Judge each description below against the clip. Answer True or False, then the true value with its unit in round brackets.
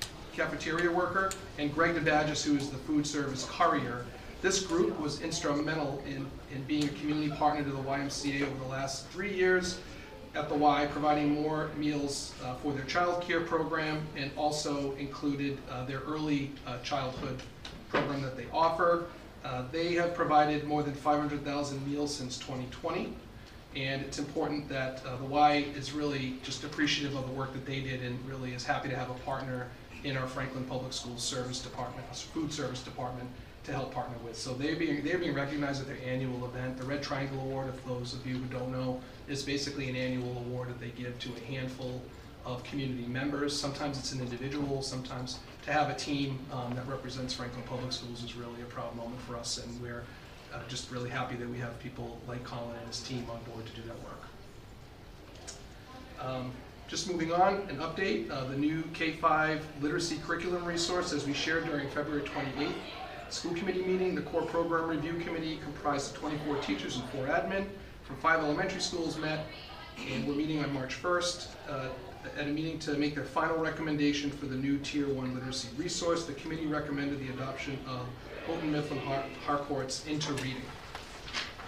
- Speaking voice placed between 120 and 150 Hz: True (140 Hz)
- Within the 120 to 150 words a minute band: False (185 wpm)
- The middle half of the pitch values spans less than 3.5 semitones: True (2.9 semitones)